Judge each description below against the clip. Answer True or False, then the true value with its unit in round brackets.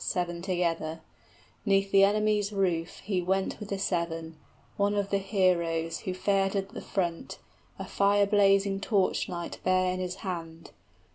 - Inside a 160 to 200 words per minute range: True (165 wpm)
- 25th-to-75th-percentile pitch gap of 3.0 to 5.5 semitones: False (2.4 semitones)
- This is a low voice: False (190 Hz)